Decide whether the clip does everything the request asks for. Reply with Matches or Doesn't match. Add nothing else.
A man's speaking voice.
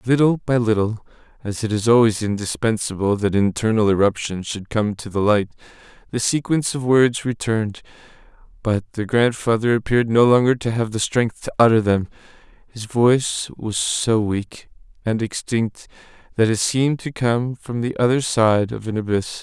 Matches